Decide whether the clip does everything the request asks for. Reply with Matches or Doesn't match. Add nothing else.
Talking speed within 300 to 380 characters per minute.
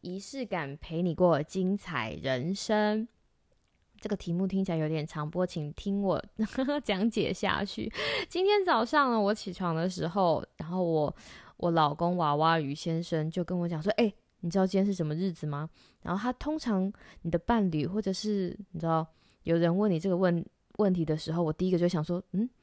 Doesn't match